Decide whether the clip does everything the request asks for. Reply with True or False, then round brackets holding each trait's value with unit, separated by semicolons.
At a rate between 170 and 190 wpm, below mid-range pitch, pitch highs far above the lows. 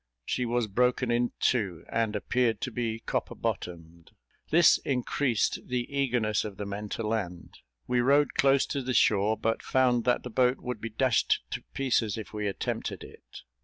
False (175 wpm; 120 Hz; 3.1 semitones)